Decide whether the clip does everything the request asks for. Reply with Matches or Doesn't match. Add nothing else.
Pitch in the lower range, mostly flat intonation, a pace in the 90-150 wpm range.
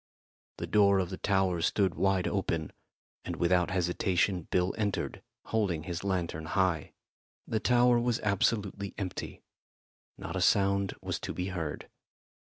Matches